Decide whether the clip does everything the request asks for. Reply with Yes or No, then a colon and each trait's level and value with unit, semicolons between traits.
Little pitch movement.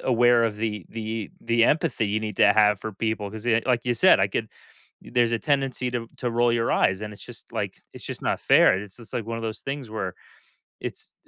Yes: narrow, 2.2 semitones